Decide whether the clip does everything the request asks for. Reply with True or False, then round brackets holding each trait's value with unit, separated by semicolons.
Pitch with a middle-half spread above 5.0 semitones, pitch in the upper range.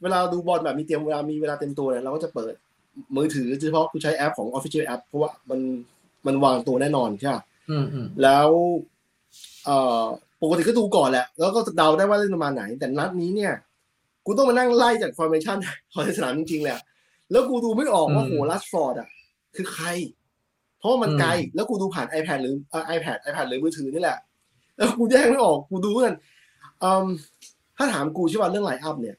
False (5.6 semitones; 160 Hz)